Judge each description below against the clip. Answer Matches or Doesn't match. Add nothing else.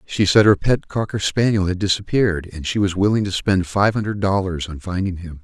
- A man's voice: Matches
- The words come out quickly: Matches